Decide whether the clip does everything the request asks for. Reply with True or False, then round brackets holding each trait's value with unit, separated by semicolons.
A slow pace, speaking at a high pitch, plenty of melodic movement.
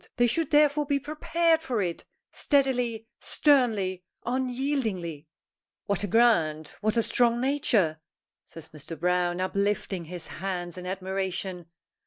True (125 wpm; 205 Hz; 6.5 semitones)